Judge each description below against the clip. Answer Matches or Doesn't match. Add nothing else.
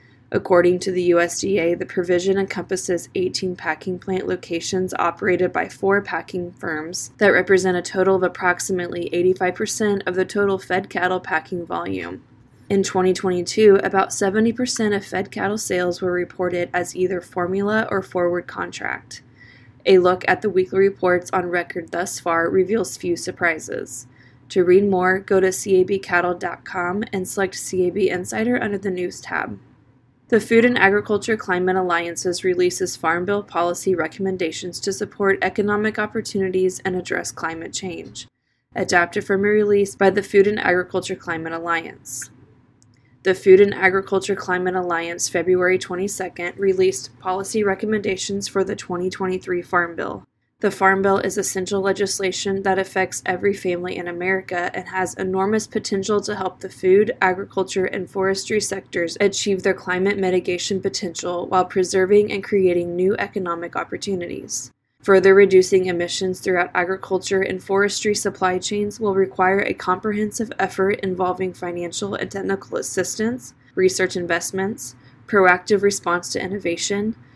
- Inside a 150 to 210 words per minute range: Doesn't match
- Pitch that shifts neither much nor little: Doesn't match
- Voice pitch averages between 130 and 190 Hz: Matches